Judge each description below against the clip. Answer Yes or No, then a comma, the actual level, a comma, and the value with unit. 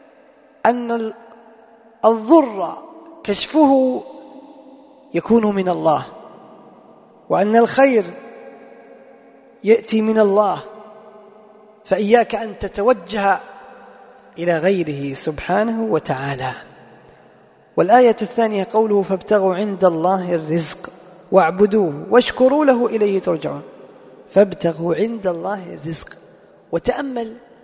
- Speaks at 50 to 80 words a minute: Yes, average, 75 wpm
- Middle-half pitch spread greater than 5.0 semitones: No, average, 4.1 semitones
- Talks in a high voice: Yes, high, 215 Hz